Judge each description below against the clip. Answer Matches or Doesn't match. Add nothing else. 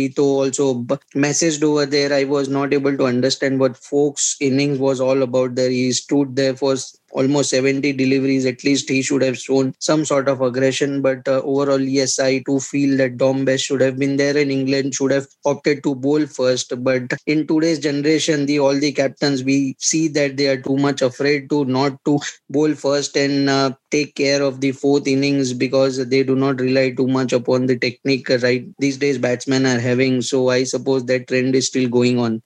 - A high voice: Doesn't match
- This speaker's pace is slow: Doesn't match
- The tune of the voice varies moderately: Doesn't match